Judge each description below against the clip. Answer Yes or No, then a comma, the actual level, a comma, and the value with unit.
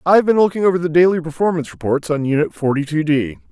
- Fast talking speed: Yes, fast, 220 wpm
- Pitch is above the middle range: No, medium, 160 Hz